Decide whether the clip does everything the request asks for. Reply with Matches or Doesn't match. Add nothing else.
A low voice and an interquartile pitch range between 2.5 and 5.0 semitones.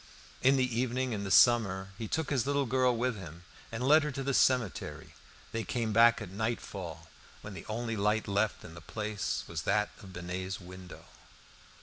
Matches